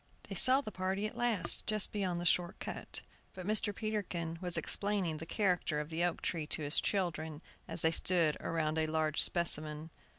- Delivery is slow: No, average, 190 wpm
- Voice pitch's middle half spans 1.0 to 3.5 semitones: No, average, 4.0 semitones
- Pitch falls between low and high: Yes, medium, 175 Hz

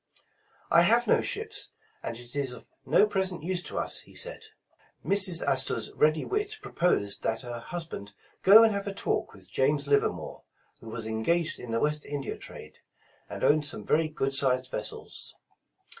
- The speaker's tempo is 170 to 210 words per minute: Yes, average, 180 wpm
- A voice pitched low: No, medium, 150 Hz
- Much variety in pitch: Yes, wide, 7.6 semitones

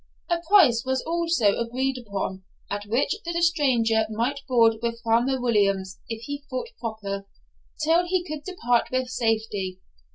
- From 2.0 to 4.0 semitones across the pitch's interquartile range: No, average, 4.6 semitones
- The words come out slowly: No, average, 150 wpm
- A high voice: Yes, high, 240 Hz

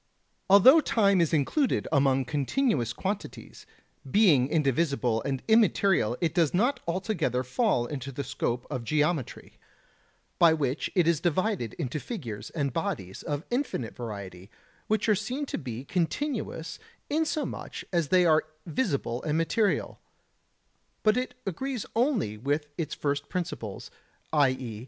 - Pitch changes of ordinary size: No, wide, 7.7 semitones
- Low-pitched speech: No, medium, 160 Hz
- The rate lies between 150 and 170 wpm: No, slow, 135 wpm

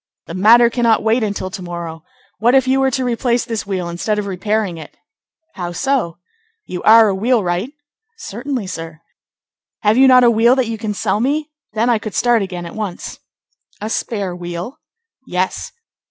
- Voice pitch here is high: Yes, high, 215 Hz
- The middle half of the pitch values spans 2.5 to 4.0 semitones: No, average, 4.7 semitones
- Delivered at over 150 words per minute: Yes, average, 180 wpm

